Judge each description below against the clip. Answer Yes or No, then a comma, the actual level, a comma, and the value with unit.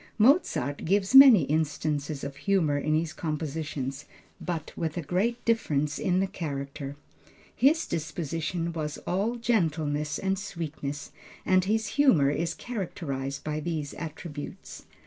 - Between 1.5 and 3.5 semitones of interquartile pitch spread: No, average, 4.7 semitones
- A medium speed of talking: No, slow, 125 wpm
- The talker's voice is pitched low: No, medium, 160 Hz